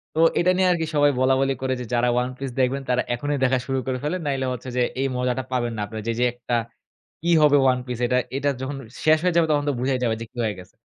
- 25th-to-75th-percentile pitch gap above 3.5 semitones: No, narrow, 2.6 semitones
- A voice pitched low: Yes, low, 130 Hz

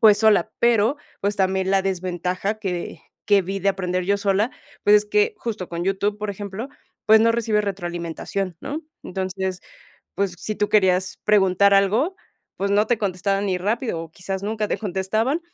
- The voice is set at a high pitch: Yes, high, 200 Hz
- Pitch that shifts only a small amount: Yes, narrow, 2.3 semitones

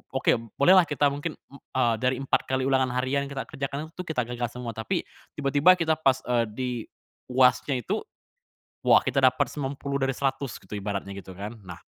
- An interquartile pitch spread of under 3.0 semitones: Yes, narrow, 2.6 semitones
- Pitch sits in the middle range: No, low, 130 Hz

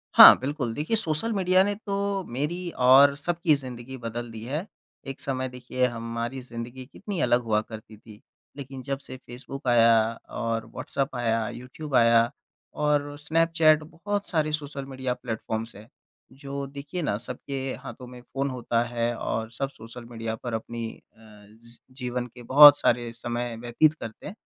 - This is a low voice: Yes, low, 130 Hz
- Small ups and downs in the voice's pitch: No, average, 4.1 semitones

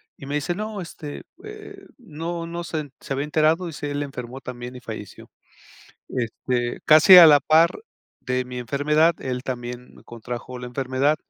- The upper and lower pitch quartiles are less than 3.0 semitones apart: No, average, 4.7 semitones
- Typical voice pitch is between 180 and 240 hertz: No, medium, 145 Hz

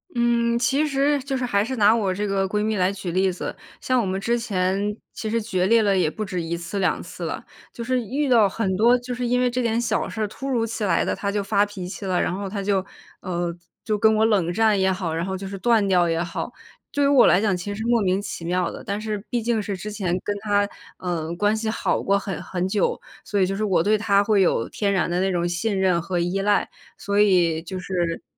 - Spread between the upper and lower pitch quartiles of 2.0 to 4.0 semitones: Yes, average, 3.3 semitones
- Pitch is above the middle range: Yes, high, 200 Hz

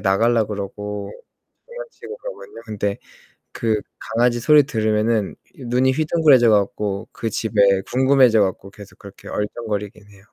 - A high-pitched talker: No, low, 110 Hz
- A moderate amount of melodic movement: Yes, average, 3.8 semitones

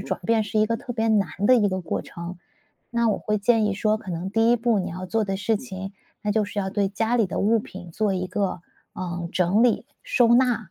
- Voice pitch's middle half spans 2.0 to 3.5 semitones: Yes, average, 3.2 semitones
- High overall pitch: Yes, high, 210 Hz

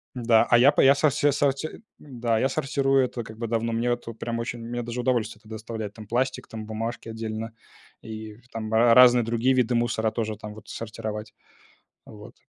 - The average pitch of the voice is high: No, low, 115 Hz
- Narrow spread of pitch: Yes, narrow, 1.9 semitones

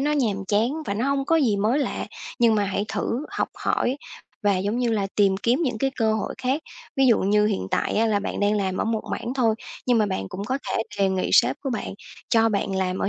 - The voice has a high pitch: Yes, high, 220 Hz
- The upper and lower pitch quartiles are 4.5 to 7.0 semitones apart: No, average, 3.8 semitones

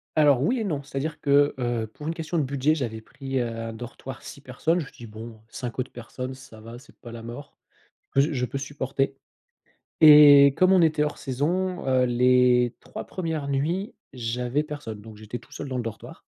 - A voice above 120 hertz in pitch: Yes, low, 135 Hz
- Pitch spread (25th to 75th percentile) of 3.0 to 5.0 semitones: Yes, average, 3.7 semitones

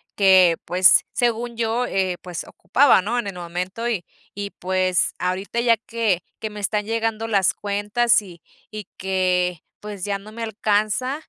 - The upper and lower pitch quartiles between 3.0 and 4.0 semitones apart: Yes, average, 3.5 semitones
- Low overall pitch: No, high, 205 Hz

